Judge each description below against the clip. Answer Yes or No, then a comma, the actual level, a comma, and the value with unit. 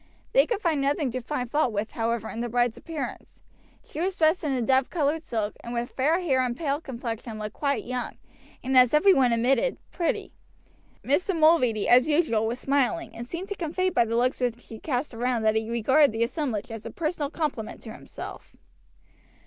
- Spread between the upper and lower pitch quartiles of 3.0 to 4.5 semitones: No, average, 4.9 semitones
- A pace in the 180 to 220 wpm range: Yes, fast, 205 wpm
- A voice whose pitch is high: Yes, very high, 255 Hz